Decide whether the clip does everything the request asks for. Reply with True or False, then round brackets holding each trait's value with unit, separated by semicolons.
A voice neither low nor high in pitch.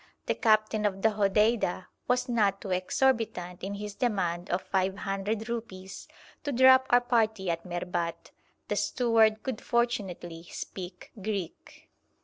False (205 Hz)